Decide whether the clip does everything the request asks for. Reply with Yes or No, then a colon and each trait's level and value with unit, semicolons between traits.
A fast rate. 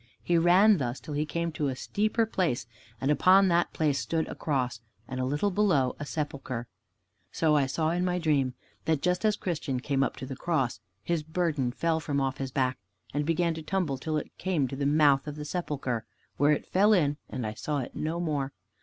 Yes: fast, 215 wpm